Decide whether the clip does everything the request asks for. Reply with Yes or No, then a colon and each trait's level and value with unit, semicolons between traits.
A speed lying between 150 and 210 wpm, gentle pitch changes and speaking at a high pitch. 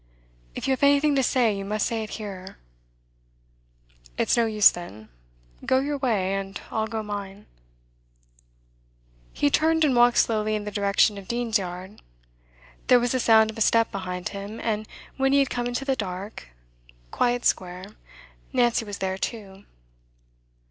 No: average, 160 wpm; average, 3.7 semitones; high, 215 Hz